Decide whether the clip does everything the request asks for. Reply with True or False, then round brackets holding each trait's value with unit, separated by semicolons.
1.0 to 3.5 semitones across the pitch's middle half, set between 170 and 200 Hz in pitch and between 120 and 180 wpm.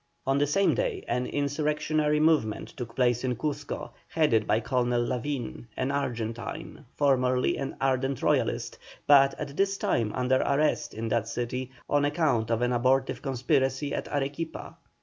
False (3.1 semitones; 135 Hz; 150 wpm)